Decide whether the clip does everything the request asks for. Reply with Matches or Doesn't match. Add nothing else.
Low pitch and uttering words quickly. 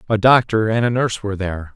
Matches